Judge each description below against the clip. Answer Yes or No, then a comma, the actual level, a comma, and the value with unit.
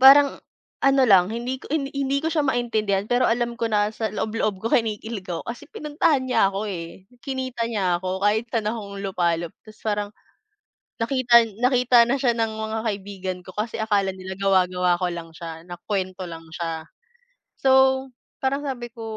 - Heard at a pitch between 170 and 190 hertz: No, high, 220 Hz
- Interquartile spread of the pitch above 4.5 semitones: Yes, average, 5.0 semitones